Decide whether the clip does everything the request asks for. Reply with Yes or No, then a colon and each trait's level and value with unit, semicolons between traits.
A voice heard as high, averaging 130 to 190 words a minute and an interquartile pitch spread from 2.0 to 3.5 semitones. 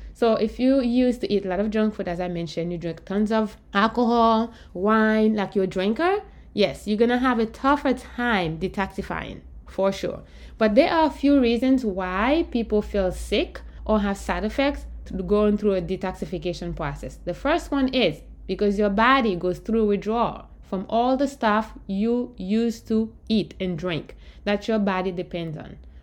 No: high, 210 Hz; average, 180 wpm; average, 4.0 semitones